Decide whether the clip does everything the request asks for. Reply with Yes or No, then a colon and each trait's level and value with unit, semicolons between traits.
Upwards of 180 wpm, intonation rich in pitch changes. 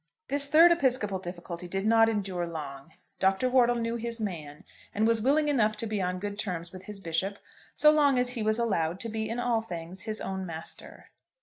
No: fast, 205 wpm; average, 4.5 semitones